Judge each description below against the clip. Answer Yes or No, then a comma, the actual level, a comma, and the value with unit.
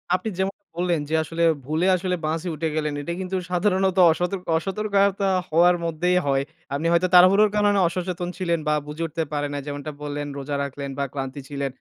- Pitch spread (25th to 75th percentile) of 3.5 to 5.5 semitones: Yes, average, 3.9 semitones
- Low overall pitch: No, medium, 170 Hz